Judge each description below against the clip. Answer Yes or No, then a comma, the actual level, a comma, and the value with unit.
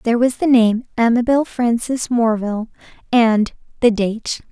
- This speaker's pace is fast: No, slow, 135 wpm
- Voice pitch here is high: Yes, high, 235 Hz